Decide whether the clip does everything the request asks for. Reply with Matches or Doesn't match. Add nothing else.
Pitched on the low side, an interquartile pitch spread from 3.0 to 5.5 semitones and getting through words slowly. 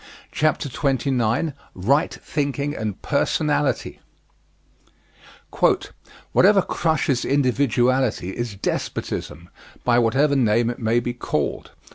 Matches